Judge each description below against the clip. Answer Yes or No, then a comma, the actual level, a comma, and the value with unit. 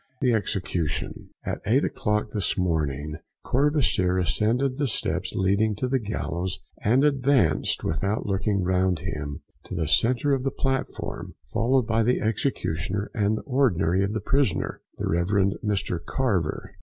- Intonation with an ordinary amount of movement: No, wide, 6.0 semitones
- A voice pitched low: Yes, low, 105 Hz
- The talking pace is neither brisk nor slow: Yes, average, 145 wpm